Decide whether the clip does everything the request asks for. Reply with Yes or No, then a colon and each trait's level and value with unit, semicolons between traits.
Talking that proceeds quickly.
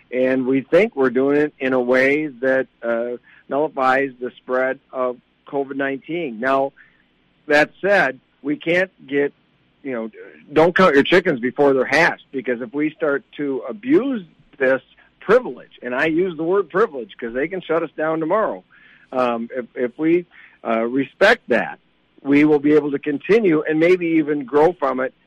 No: average, 170 wpm